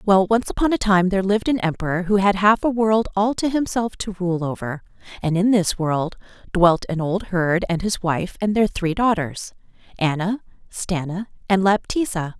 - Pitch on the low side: No, high, 195 Hz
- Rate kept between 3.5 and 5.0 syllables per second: Yes, 4.9 syllables/s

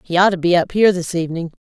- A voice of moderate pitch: Yes, medium, 175 Hz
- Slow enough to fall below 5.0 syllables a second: No, 7.6 syllables/s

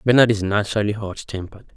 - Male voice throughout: Yes, male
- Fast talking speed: No, average, 170 wpm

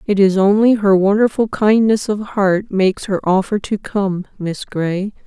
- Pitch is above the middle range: Yes, high, 200 Hz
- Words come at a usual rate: Yes, average, 170 wpm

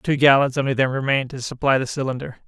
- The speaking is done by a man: Yes, male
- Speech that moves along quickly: Yes, fast, 220 wpm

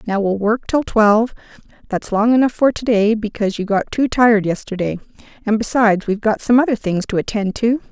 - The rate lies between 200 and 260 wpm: Yes, fast, 205 wpm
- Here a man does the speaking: No, female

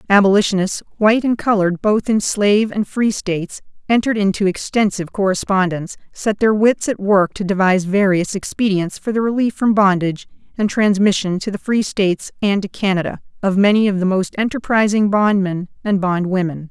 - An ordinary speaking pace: Yes, average, 165 wpm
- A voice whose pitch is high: Yes, high, 200 Hz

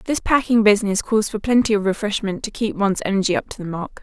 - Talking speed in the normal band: No, fast, 240 wpm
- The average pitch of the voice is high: Yes, high, 210 Hz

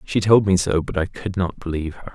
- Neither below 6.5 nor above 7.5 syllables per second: No, 5.9 syllables/s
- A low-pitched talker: Yes, very low, 95 Hz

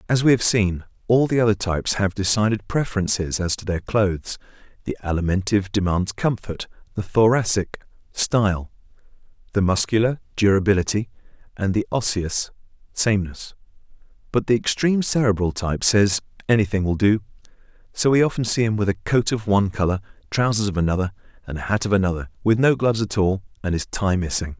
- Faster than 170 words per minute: No, average, 155 wpm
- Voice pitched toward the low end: Yes, low, 100 Hz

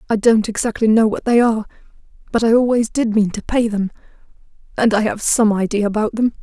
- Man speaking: No, female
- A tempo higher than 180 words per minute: Yes, fast, 205 wpm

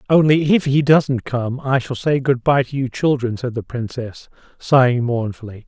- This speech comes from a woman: No, male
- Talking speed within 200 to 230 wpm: No, average, 190 wpm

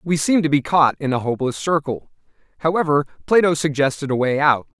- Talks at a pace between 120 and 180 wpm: No, average, 190 wpm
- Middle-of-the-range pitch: Yes, medium, 150 Hz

